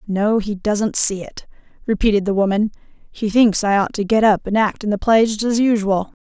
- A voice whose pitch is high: Yes, high, 210 Hz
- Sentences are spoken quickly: Yes, fast, 220 wpm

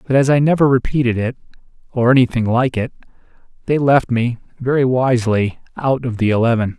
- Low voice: Yes, low, 125 Hz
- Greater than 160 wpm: No, average, 150 wpm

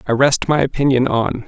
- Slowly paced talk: No, fast, 205 wpm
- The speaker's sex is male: Yes, male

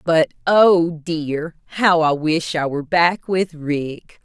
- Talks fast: No, average, 155 wpm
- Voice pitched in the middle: Yes, medium, 165 Hz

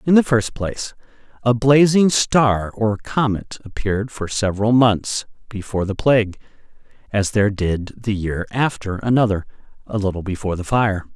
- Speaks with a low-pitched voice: Yes, low, 110 Hz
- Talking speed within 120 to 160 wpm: Yes, average, 150 wpm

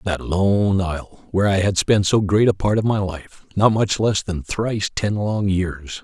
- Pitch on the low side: Yes, low, 100 Hz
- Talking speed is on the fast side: Yes, fast, 210 wpm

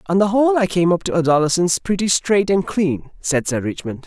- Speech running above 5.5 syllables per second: Yes, 5.7 syllables/s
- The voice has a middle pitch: Yes, medium, 180 Hz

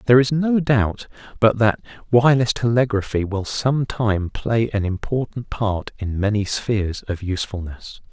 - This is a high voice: No, low, 110 Hz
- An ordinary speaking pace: Yes, average, 150 wpm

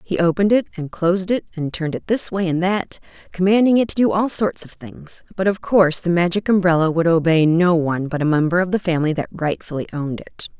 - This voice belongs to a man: No, female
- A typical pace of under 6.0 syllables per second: No, 6.1 syllables/s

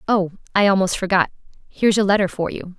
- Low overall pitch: No, high, 195 Hz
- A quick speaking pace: No, average, 170 wpm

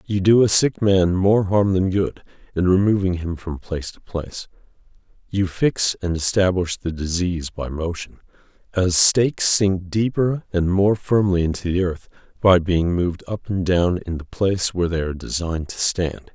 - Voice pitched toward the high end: No, very low, 90 Hz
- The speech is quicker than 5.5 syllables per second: No, 4.9 syllables/s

